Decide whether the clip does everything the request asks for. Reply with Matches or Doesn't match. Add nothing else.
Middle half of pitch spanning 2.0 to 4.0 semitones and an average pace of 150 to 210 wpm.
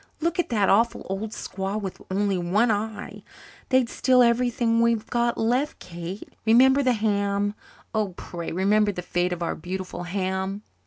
Matches